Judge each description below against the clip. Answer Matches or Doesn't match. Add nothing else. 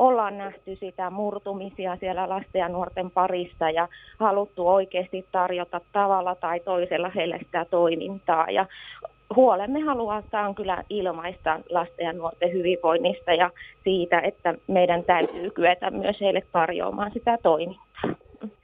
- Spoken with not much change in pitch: Matches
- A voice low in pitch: Doesn't match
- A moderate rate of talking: Matches